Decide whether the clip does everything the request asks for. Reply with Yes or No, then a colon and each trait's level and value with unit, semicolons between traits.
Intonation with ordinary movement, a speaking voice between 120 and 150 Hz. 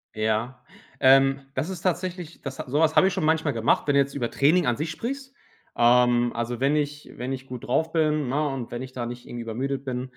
Yes: average, 4.1 semitones; low, 135 Hz